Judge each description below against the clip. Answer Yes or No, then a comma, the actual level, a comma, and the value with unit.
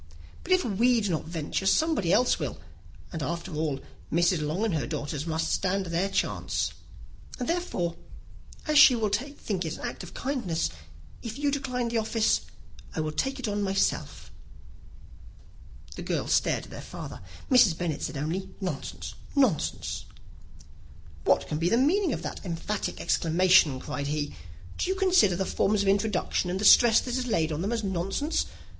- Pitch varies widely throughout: Yes, wide, 6.8 semitones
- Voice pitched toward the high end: Yes, high, 195 Hz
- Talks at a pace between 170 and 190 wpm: Yes, average, 175 wpm